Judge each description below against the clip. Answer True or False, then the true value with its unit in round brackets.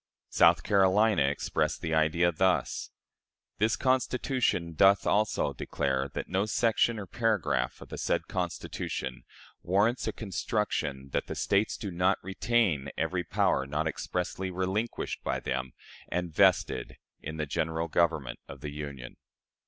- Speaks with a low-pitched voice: True (90 Hz)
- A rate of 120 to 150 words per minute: True (135 wpm)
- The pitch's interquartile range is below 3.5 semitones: False (5.4 semitones)